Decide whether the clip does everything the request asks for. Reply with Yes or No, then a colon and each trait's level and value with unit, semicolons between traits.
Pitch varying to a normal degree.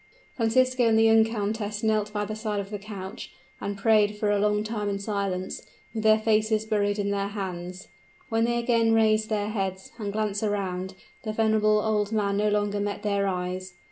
No: narrow, 1.5 semitones